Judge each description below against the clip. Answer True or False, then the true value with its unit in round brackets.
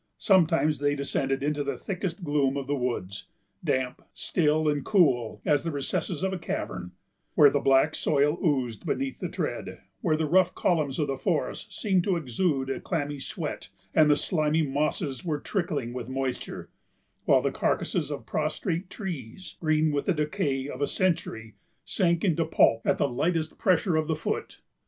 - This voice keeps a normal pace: True (175 wpm)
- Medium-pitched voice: True (150 Hz)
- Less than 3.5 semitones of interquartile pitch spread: False (3.9 semitones)